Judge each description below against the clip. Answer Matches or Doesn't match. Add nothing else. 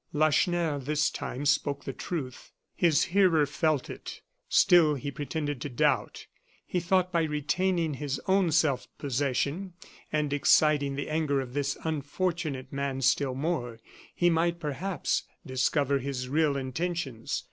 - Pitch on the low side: Doesn't match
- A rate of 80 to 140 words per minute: Matches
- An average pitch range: Matches